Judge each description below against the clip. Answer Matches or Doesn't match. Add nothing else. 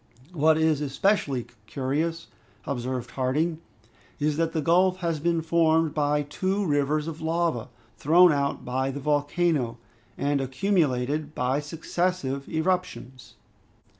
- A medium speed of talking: Doesn't match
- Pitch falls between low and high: Matches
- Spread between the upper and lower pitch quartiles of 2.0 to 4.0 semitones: Matches